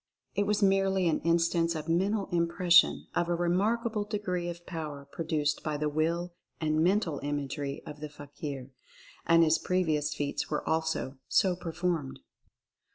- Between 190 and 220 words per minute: No, average, 155 wpm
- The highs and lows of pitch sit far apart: No, average, 3.2 semitones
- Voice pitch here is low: No, medium, 165 Hz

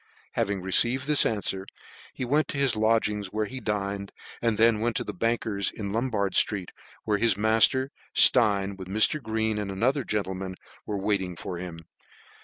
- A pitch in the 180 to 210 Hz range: No, low, 105 Hz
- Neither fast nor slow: Yes, average, 170 wpm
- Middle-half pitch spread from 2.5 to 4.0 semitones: Yes, average, 2.8 semitones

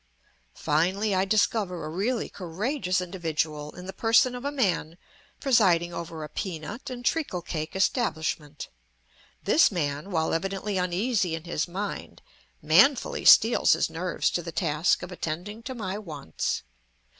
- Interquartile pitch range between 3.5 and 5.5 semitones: Yes, average, 4.8 semitones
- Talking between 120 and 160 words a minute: Yes, average, 145 wpm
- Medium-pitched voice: Yes, medium, 180 Hz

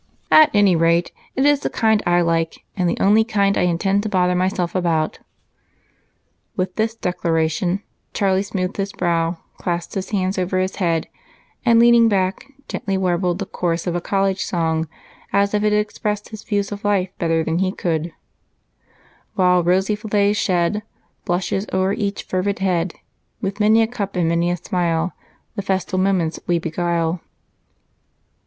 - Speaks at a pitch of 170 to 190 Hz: Yes, medium, 185 Hz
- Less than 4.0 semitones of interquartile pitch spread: Yes, average, 2.8 semitones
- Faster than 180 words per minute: No, average, 165 wpm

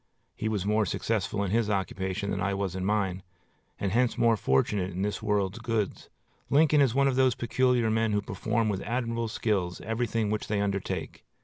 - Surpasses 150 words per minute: Yes, average, 190 wpm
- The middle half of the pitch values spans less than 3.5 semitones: Yes, average, 2.8 semitones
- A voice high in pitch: No, low, 105 Hz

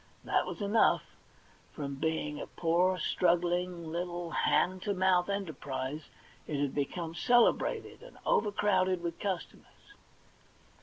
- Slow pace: Yes, slow, 115 wpm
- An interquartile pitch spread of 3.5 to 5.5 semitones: No, average, 2.7 semitones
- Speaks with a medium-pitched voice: Yes, medium, 175 Hz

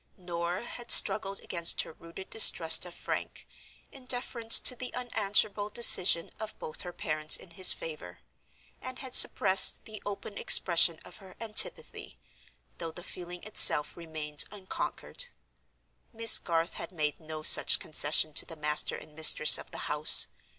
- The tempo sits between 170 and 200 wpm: No, average, 150 wpm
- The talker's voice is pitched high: No, medium, 175 Hz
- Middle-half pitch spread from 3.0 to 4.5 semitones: No, average, 5.2 semitones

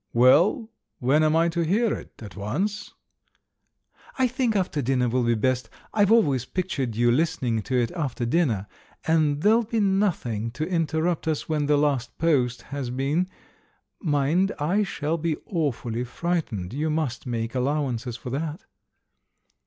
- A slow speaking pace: No, average, 160 wpm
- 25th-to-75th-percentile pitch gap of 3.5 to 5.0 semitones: No, wide, 5.6 semitones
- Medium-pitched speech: Yes, medium, 150 Hz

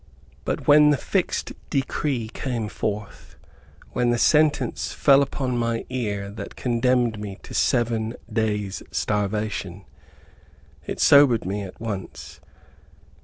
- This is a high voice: No, low, 115 Hz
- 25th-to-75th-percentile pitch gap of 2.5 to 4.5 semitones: Yes, average, 3.6 semitones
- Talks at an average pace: No, slow, 120 wpm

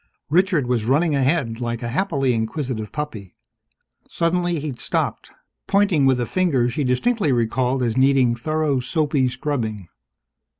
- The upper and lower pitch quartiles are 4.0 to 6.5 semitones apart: Yes, average, 4.5 semitones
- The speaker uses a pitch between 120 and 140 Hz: Yes, low, 135 Hz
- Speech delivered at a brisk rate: No, slow, 135 wpm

